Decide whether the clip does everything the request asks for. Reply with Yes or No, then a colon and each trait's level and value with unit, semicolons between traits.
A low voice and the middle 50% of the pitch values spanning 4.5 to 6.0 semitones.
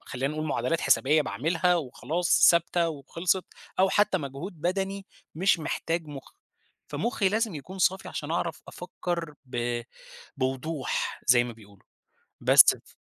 No: medium, 165 Hz; average, 4.9 semitones